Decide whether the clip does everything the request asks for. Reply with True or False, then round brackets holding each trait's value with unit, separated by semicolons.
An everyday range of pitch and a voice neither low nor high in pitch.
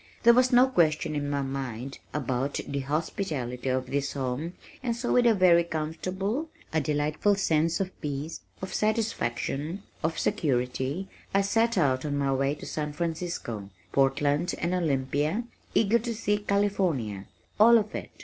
False (6.4 semitones; 155 Hz)